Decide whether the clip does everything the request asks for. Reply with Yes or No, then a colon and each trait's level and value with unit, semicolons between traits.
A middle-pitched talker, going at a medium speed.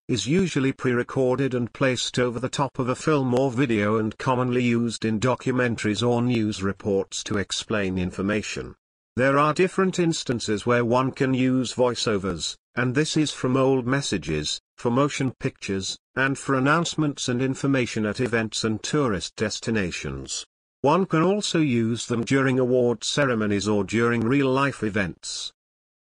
No: low, 125 Hz; average, 150 wpm